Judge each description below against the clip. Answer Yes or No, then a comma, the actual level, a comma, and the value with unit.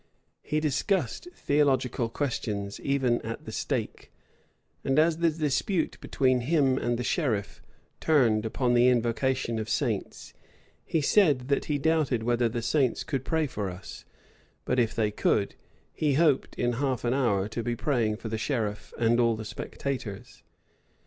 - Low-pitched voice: Yes, low, 125 Hz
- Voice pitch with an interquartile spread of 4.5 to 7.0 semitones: No, average, 4.1 semitones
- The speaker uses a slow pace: No, average, 155 wpm